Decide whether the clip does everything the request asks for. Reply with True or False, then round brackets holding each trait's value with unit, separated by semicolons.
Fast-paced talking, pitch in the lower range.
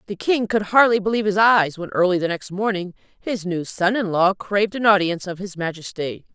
False (215 wpm; 195 Hz)